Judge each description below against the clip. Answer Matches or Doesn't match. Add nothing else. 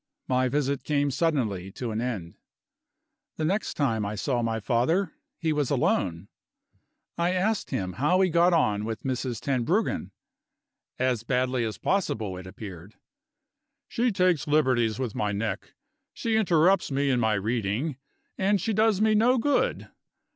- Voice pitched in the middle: Doesn't match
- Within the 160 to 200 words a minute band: Doesn't match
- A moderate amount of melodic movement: Doesn't match